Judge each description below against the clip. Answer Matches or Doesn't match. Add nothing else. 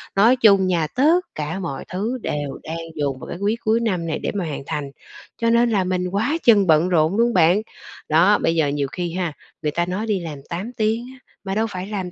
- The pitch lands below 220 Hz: Matches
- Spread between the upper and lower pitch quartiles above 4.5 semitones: Matches